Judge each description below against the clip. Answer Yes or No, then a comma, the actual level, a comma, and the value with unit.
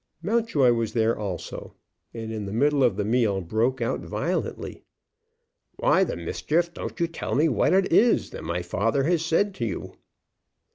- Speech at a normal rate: Yes, average, 175 wpm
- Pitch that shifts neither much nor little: No, wide, 7.4 semitones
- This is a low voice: Yes, low, 120 Hz